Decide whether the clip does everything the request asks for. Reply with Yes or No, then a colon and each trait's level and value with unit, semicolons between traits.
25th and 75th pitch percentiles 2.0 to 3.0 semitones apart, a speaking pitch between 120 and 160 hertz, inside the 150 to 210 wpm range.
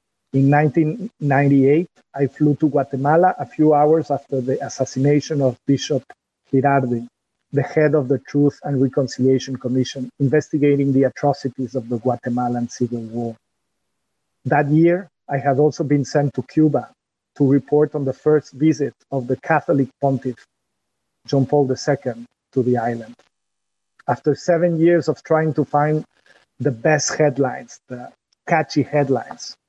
No: narrow, 2.6 semitones; medium, 140 Hz; average, 140 wpm